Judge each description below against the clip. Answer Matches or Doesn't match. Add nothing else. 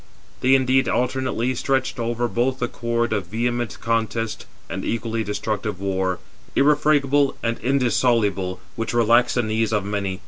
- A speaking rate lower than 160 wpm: Matches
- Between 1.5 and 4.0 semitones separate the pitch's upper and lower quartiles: Matches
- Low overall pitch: Matches